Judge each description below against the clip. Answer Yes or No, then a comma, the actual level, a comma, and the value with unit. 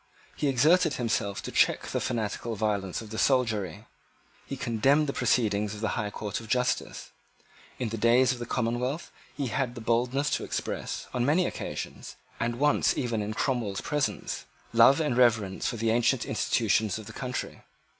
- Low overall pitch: Yes, low, 120 Hz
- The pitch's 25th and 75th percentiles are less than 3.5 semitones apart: Yes, average, 3.1 semitones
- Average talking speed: Yes, average, 175 wpm